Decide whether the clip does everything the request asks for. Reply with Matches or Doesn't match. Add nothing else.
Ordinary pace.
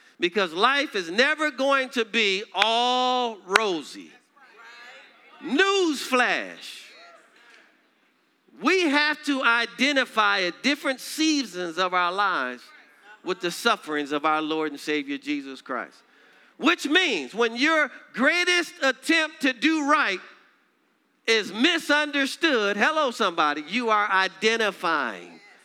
Doesn't match